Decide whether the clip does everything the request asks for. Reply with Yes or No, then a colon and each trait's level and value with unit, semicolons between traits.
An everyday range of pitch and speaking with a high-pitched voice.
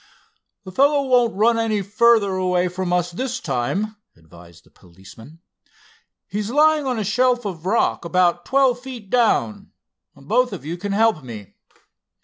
No: wide, 5.9 semitones; high, 200 Hz